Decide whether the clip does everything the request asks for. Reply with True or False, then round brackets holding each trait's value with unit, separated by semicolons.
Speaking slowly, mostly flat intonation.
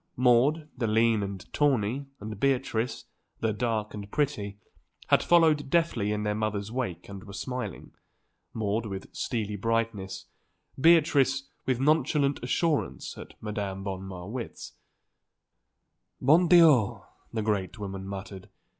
False (125 wpm; 5.1 semitones)